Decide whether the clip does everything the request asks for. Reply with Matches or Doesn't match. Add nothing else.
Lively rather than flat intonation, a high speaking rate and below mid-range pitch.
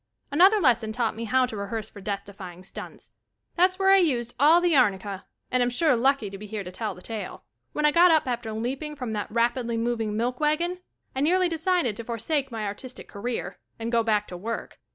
Doesn't match